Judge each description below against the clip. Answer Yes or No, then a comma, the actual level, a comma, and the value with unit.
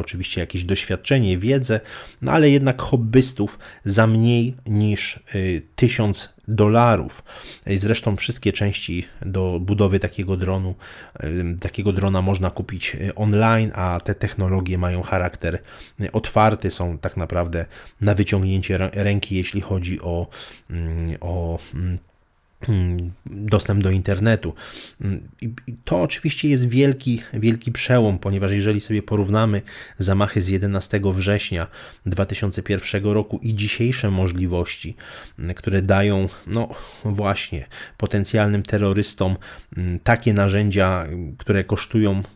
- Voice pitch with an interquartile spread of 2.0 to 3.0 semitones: Yes, average, 2.7 semitones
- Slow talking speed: Yes, slow, 105 wpm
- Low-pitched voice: Yes, low, 100 Hz